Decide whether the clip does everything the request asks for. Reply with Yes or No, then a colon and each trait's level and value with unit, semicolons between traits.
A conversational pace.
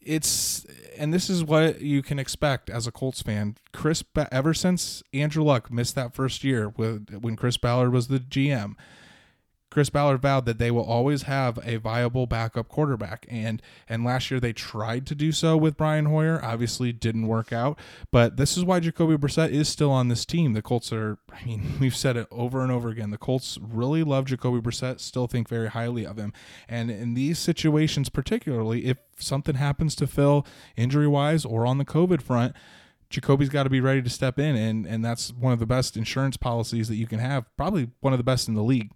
No: fast, 210 wpm